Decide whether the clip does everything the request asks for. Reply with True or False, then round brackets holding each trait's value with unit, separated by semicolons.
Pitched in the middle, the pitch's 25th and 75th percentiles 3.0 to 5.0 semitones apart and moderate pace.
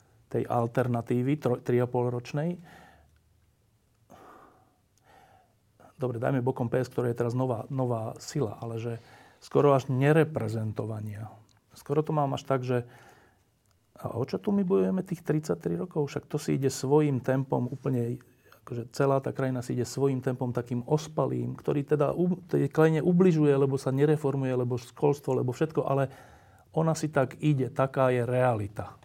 False (130 Hz; 3.5 semitones; 145 wpm)